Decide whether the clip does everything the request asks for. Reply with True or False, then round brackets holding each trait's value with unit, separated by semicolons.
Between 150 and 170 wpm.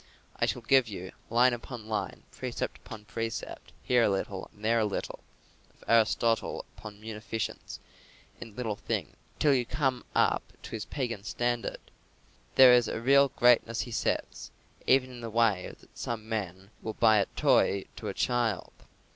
True (165 wpm)